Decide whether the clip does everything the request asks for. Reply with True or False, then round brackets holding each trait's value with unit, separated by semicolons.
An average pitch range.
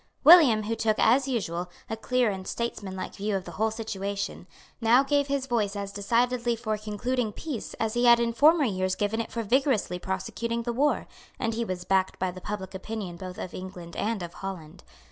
True (3.9 semitones)